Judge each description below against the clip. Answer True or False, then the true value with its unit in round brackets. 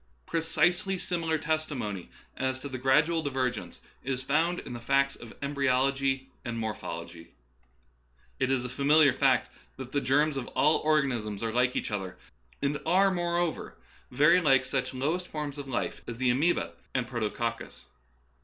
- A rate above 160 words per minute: False (155 wpm)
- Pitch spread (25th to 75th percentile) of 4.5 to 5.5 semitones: False (3.7 semitones)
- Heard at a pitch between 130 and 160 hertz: True (135 Hz)